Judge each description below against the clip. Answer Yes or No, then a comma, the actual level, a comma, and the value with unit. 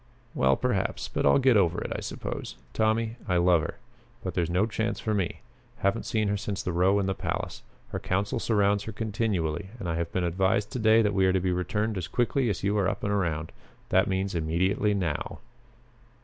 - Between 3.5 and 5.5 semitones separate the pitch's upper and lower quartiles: No, average, 3.1 semitones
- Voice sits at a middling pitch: No, low, 100 Hz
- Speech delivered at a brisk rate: Yes, fast, 215 wpm